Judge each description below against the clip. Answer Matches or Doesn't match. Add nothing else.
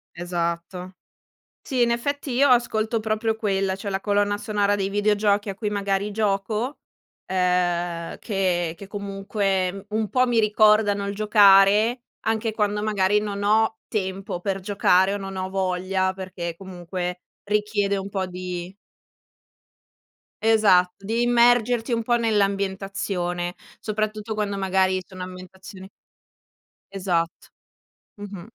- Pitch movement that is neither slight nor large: Doesn't match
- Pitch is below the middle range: Doesn't match